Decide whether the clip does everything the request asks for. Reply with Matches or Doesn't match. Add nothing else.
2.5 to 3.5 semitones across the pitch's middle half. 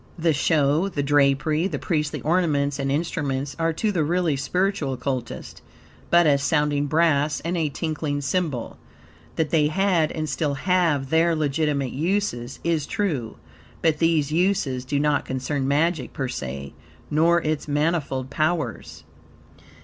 Matches